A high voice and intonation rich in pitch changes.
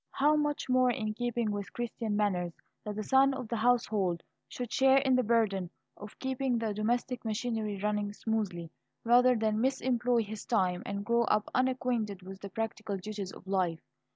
No: high, 220 Hz; average, 3.4 semitones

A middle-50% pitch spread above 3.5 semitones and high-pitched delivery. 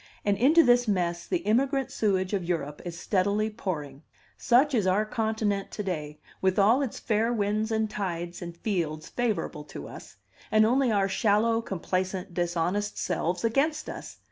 Yes: average, 4.3 semitones; high, 205 Hz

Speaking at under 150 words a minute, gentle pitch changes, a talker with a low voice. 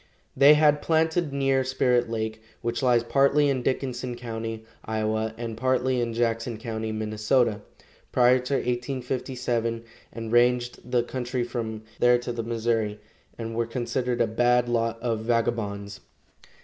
Yes: average, 140 wpm; narrow, 2.0 semitones; low, 120 Hz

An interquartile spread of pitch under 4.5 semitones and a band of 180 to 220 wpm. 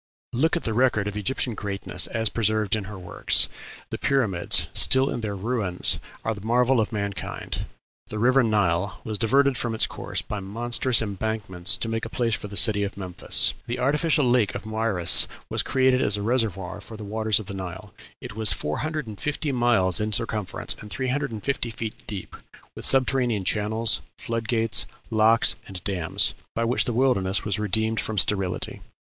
Yes: average, 3.1 semitones; average, 190 wpm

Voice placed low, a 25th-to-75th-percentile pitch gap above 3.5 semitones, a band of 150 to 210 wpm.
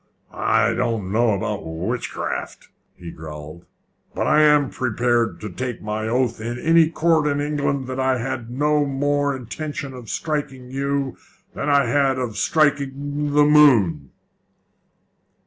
No: low, 130 Hz; average, 4.0 semitones; average, 140 wpm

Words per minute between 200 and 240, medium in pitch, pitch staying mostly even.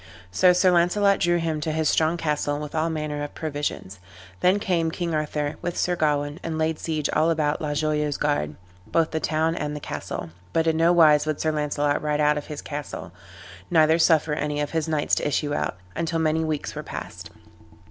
Yes: fast, 205 wpm; medium, 155 Hz; narrow, 1.8 semitones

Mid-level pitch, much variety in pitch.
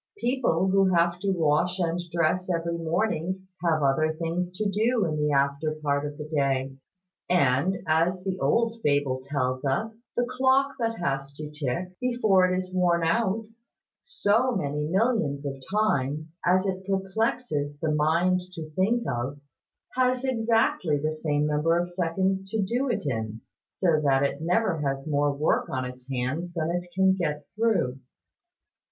No: medium, 170 Hz; average, 4.8 semitones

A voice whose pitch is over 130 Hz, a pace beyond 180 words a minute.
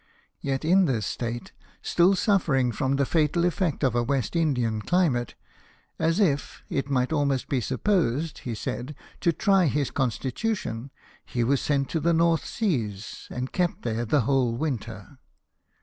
No: medium, 140 Hz; average, 155 wpm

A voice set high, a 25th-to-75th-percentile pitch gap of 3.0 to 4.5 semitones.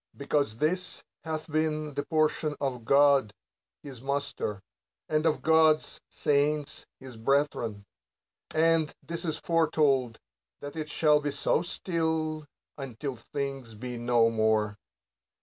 No: medium, 145 Hz; average, 3.8 semitones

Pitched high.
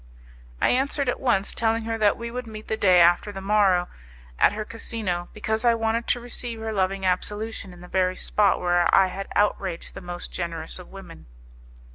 Yes: high, 205 Hz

